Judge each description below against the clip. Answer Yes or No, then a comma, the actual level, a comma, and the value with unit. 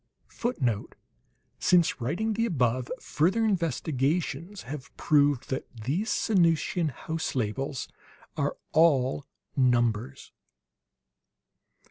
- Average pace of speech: No, slow, 85 wpm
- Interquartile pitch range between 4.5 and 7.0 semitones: Yes, average, 5.3 semitones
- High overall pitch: No, medium, 145 Hz